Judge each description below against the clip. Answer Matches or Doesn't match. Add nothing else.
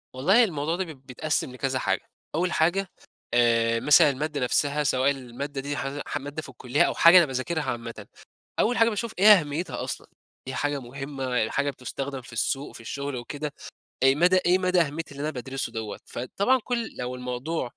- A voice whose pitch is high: Doesn't match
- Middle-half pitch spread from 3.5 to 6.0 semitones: Matches